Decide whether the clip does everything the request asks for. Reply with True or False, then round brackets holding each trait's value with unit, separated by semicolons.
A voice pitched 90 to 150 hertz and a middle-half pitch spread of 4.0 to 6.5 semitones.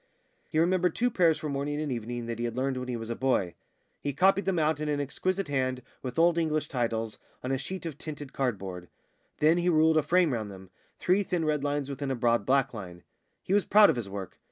True (140 Hz; 5.2 semitones)